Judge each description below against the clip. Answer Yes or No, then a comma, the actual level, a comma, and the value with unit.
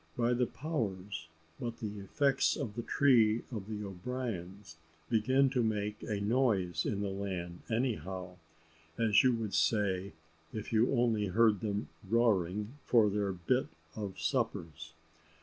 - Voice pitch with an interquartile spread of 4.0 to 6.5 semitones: No, average, 3.5 semitones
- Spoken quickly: No, average, 140 wpm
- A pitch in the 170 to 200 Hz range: No, low, 105 Hz